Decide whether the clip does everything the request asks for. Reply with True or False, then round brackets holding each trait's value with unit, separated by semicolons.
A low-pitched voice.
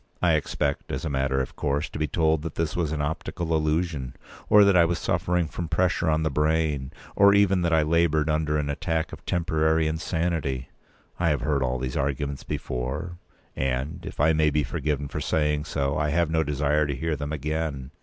True (75 Hz)